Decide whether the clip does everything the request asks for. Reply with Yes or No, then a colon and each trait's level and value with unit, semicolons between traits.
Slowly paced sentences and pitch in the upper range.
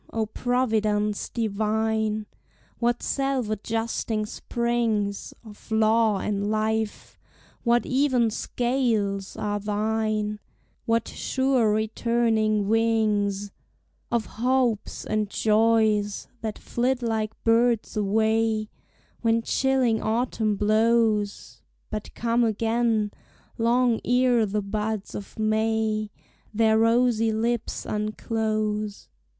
Yes: slow, 95 wpm; high, 220 Hz